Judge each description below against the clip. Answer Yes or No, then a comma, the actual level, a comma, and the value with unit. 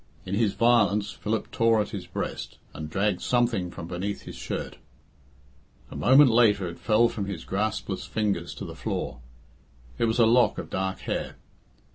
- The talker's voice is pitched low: Yes, low, 105 Hz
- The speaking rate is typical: Yes, average, 170 wpm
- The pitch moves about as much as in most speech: Yes, average, 3.3 semitones